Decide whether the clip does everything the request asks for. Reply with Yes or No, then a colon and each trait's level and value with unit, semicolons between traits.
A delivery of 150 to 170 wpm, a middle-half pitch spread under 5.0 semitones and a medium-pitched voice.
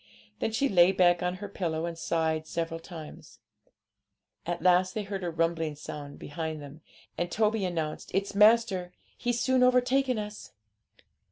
Yes: average, 155 wpm; average, 4.3 semitones; medium, 180 Hz